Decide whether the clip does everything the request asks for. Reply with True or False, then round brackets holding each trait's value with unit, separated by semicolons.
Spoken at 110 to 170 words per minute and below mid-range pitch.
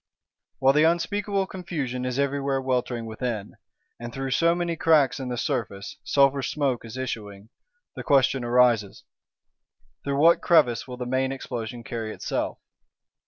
True (145 wpm; 130 Hz)